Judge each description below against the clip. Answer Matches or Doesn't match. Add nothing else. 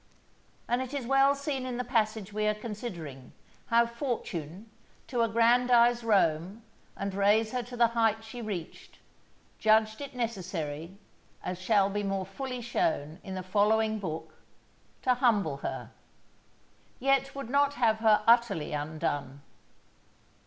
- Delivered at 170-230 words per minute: Doesn't match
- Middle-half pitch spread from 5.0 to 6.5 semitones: Doesn't match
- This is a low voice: Doesn't match